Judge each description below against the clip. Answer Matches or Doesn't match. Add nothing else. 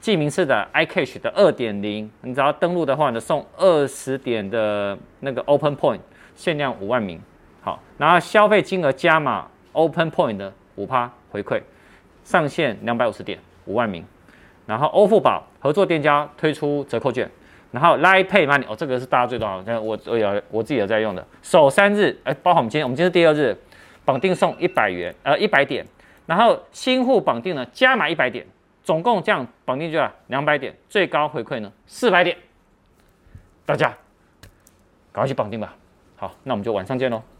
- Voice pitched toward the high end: Doesn't match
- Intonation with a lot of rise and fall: Matches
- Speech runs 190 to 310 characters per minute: Doesn't match